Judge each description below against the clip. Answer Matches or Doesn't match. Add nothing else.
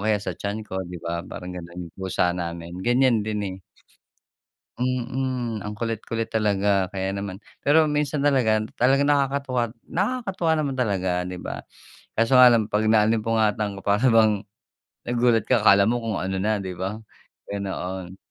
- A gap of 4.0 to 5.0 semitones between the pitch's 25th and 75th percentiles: Matches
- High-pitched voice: Doesn't match